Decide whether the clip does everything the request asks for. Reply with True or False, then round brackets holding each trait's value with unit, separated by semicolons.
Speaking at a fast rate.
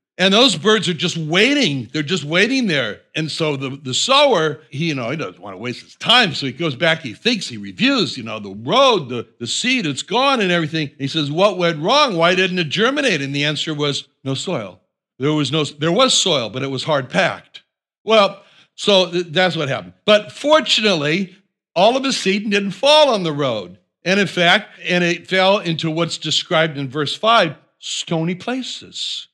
True (210 wpm)